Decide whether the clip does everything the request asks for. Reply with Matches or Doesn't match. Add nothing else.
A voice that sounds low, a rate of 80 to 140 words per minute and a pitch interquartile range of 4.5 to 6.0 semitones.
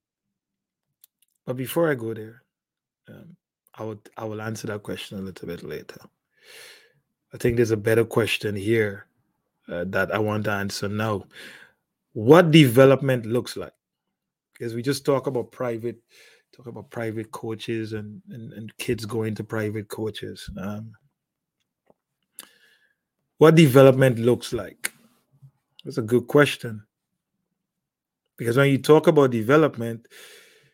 Doesn't match